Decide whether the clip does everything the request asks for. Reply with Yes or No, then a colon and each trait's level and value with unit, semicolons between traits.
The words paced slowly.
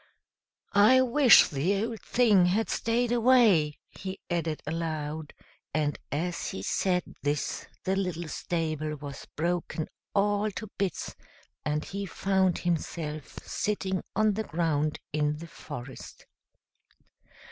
Yes: slow, 120 wpm